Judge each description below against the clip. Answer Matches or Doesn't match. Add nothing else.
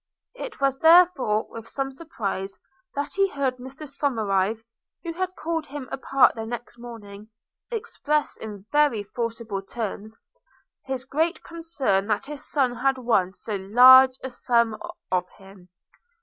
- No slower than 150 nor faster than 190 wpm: Doesn't match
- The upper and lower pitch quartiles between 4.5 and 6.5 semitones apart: Matches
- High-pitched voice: Matches